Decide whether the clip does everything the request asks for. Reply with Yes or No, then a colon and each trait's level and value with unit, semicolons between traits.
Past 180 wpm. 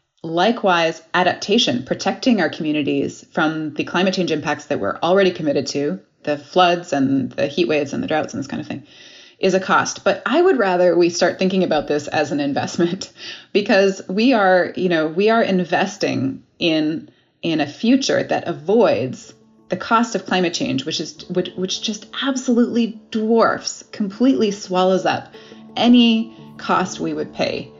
No: average, 170 wpm